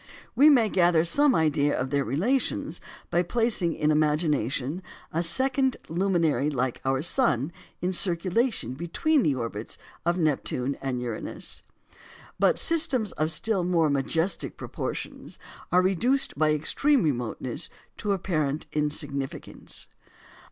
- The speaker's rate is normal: No, slow, 125 wpm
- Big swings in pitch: Yes, wide, 5.9 semitones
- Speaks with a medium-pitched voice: Yes, medium, 165 Hz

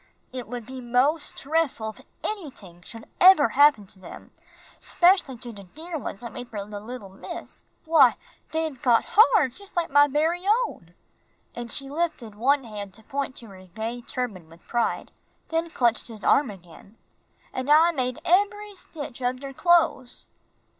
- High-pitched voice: Yes, very high, 255 Hz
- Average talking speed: Yes, average, 165 wpm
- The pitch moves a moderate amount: No, wide, 6.3 semitones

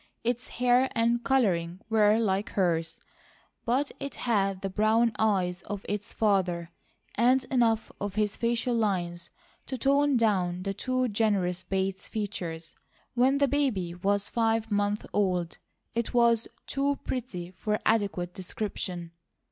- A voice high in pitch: Yes, high, 210 Hz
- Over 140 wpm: No, slow, 135 wpm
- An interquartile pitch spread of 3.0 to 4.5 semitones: Yes, average, 4.1 semitones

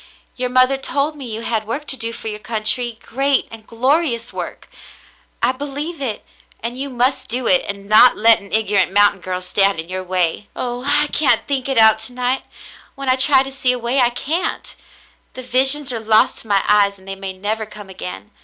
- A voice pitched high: Yes, high, 235 Hz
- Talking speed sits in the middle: No, fast, 210 wpm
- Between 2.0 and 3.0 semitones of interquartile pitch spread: No, average, 4.3 semitones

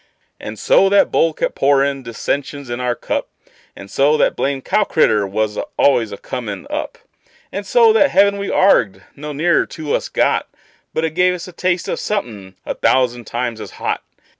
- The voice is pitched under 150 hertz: Yes, medium, 140 Hz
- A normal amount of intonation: No, wide, 7.5 semitones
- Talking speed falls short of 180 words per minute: No, average, 190 wpm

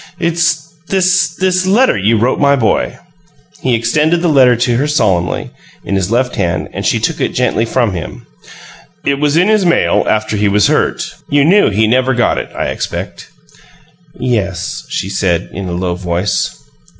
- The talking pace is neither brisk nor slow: Yes, average, 175 wpm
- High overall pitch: No, low, 125 Hz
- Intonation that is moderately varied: No, wide, 8.4 semitones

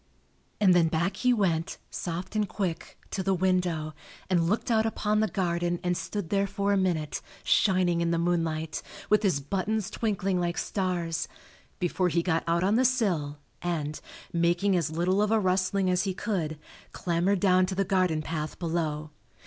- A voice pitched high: No, medium, 180 Hz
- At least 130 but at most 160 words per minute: No, average, 175 wpm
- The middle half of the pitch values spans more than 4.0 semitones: No, average, 2.9 semitones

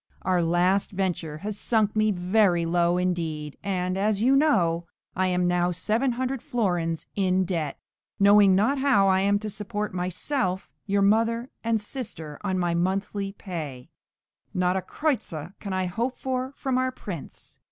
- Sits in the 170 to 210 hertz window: Yes, high, 190 Hz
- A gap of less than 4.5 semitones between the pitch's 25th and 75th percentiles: Yes, average, 3.6 semitones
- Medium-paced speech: Yes, average, 160 wpm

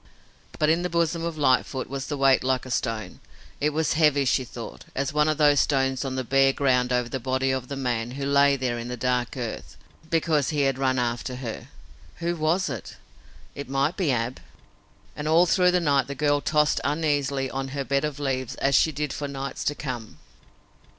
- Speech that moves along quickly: Yes, fast, 210 wpm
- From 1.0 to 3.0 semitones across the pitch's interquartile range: Yes, narrow, 2.6 semitones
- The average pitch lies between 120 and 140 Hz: Yes, low, 135 Hz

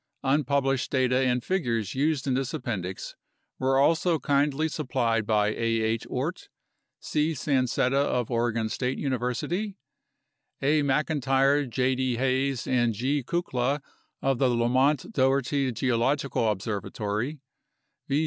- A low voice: Yes, low, 130 Hz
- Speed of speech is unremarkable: No, slow, 120 wpm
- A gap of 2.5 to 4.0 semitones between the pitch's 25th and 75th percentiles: Yes, average, 2.9 semitones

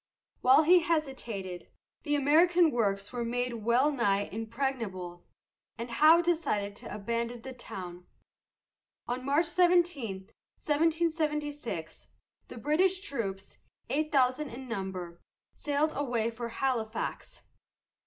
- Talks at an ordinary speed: No, slow, 110 wpm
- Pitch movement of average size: No, wide, 5.9 semitones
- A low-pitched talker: No, very high, 250 Hz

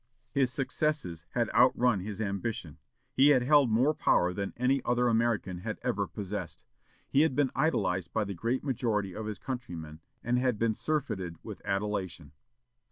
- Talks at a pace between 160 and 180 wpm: Yes, average, 165 wpm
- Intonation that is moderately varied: Yes, average, 5.0 semitones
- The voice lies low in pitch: Yes, low, 115 Hz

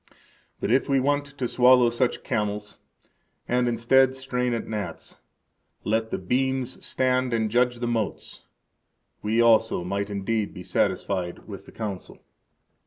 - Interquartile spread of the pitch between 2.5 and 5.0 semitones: Yes, average, 3.4 semitones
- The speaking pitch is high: No, low, 115 Hz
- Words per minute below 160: Yes, average, 140 wpm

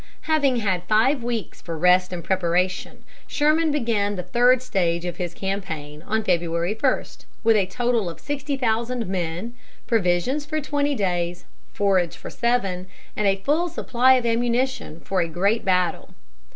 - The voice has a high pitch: Yes, high, 205 Hz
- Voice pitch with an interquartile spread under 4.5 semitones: No, wide, 5.6 semitones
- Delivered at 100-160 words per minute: Yes, average, 155 wpm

